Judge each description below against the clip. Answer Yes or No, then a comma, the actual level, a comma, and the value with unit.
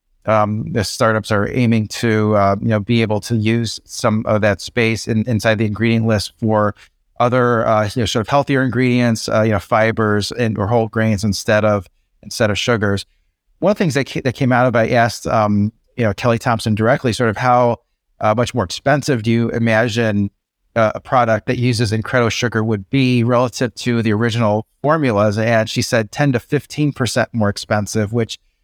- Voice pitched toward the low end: Yes, low, 115 Hz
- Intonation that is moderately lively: No, narrow, 2.3 semitones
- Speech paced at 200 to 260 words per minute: Yes, fast, 205 wpm